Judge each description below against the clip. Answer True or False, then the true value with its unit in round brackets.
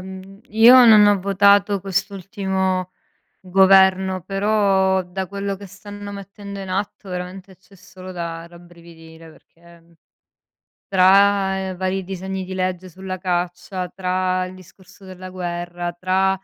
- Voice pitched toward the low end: False (190 Hz)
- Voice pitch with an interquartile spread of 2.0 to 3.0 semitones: False (1.3 semitones)